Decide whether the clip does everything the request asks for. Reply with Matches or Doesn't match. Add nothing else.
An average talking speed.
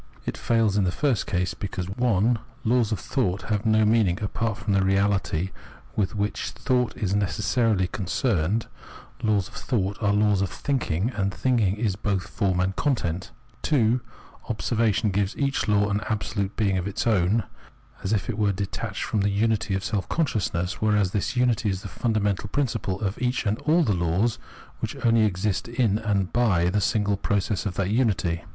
Matches